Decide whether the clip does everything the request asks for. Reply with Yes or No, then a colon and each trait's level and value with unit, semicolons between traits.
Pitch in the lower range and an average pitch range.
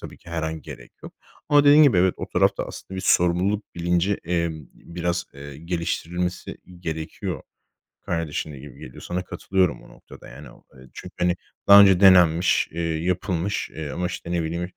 No: very low, 85 Hz; narrow, 2.3 semitones